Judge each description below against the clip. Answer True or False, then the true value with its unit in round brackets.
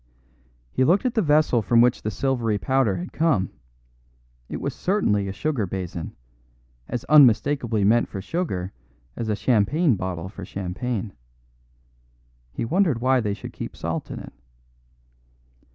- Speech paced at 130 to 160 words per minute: True (145 wpm)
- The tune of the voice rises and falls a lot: True (6.2 semitones)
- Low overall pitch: True (115 Hz)